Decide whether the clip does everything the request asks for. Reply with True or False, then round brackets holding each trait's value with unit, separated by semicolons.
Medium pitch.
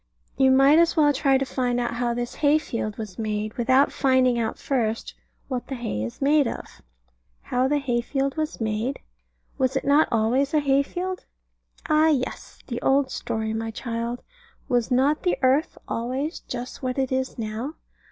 False (260 Hz)